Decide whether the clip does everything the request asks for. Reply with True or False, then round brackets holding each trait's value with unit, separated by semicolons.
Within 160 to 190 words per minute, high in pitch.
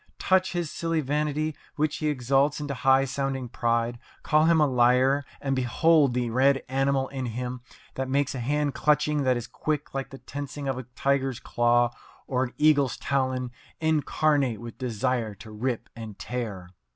False (170 wpm; 135 Hz)